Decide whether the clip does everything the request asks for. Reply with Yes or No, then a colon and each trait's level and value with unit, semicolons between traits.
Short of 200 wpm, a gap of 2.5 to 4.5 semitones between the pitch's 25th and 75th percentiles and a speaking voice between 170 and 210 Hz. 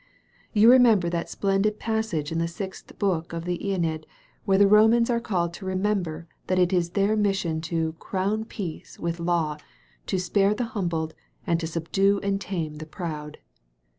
Yes: average, 170 wpm; average, 3.4 semitones; medium, 185 Hz